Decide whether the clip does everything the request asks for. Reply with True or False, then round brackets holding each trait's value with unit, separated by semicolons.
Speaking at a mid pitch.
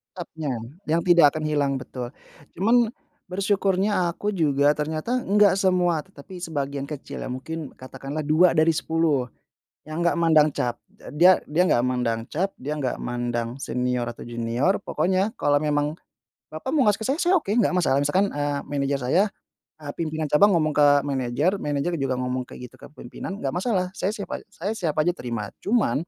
True (155 Hz)